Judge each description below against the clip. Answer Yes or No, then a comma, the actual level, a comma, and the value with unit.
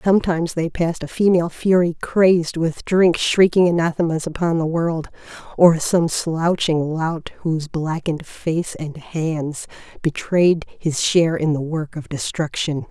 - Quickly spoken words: No, average, 145 wpm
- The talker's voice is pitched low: No, medium, 165 Hz